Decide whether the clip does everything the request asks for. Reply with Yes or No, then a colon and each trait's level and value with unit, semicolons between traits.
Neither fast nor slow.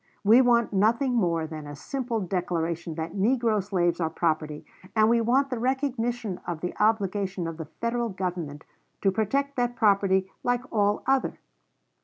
Yes: average, 160 wpm